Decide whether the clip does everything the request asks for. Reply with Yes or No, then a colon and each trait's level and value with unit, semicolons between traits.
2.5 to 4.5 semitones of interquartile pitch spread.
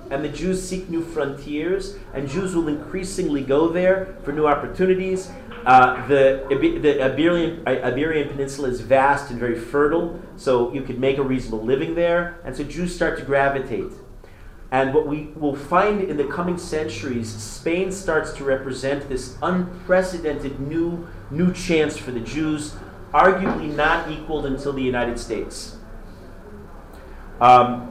No: average, 4.9 semitones